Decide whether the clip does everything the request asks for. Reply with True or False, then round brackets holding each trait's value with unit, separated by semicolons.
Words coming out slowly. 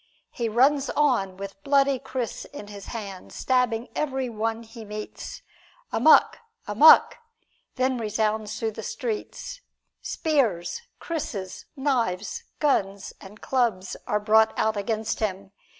True (120 wpm)